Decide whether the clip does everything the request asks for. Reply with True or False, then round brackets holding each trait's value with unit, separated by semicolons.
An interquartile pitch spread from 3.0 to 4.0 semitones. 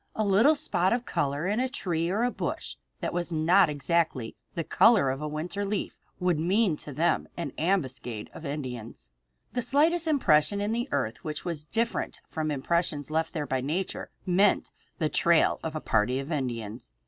False (5.6 semitones)